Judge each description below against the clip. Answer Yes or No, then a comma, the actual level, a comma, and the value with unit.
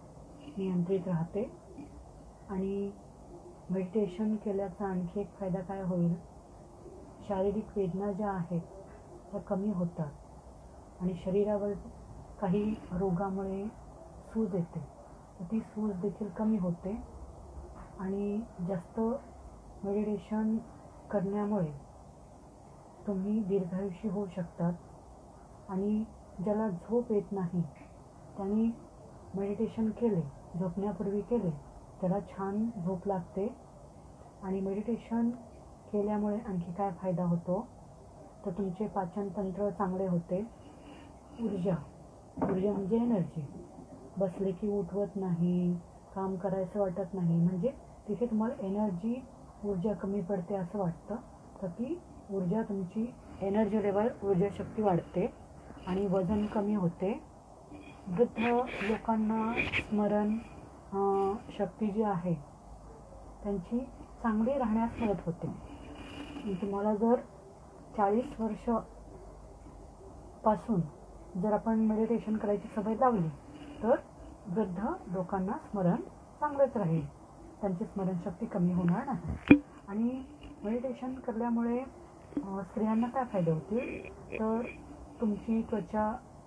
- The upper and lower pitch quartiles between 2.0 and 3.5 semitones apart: Yes, narrow, 2.6 semitones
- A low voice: No, high, 200 Hz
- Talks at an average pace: Yes, average, 95 wpm